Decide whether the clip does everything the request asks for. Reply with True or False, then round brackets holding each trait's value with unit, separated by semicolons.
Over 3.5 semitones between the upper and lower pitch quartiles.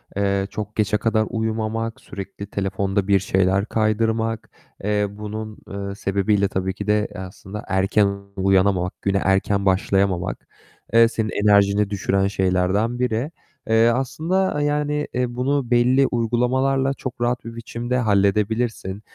False (3.1 semitones)